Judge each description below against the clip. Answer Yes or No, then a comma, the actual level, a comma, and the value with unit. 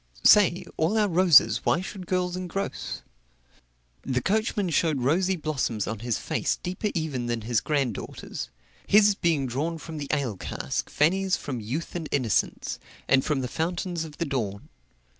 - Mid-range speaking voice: Yes, medium, 160 Hz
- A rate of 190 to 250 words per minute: No, average, 160 wpm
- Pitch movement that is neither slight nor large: No, wide, 6.1 semitones